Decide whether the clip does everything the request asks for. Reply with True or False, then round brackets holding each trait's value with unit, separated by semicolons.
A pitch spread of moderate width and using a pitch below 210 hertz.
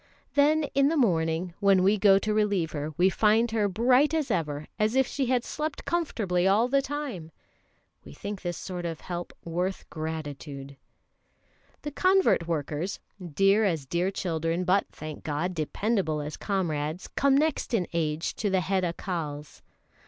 False (5.7 semitones; 185 Hz)